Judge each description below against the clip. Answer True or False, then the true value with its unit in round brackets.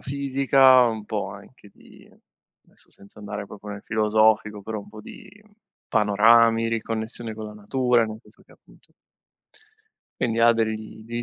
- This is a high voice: False (110 Hz)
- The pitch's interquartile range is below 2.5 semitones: True (1.8 semitones)